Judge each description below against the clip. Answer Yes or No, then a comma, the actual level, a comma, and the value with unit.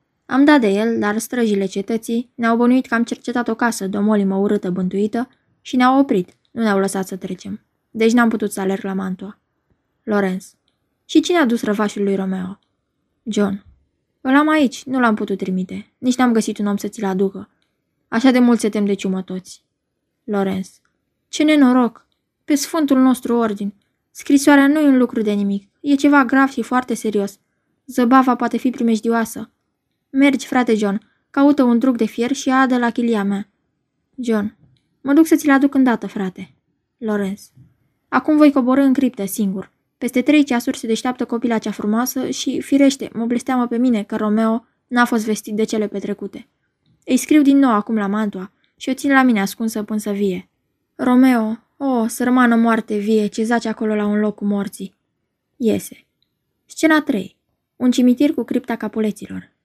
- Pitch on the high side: Yes, high, 230 Hz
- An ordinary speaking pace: No, fast, 175 wpm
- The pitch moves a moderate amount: Yes, average, 4.0 semitones